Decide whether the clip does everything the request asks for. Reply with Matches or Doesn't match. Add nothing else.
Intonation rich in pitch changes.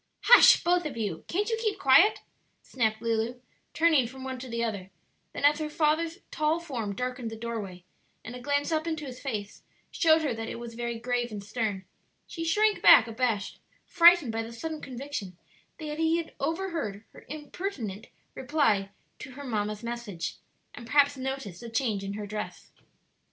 Matches